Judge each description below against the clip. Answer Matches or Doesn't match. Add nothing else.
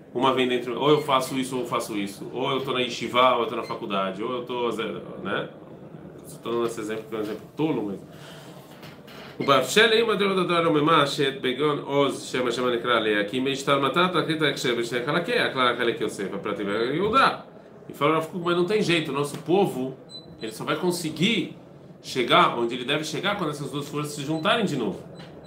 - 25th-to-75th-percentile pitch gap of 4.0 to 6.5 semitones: Matches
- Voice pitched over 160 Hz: Doesn't match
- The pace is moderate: Doesn't match